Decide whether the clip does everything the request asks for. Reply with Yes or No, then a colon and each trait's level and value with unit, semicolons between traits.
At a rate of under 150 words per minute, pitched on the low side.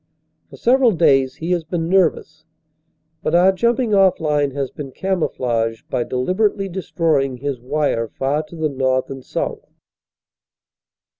No: average, 140 wpm; medium, 155 Hz